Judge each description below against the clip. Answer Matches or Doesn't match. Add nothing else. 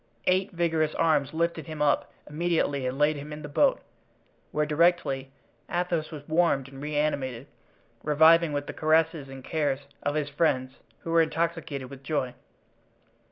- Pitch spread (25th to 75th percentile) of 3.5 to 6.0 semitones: Doesn't match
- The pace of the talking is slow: Doesn't match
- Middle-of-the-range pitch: Matches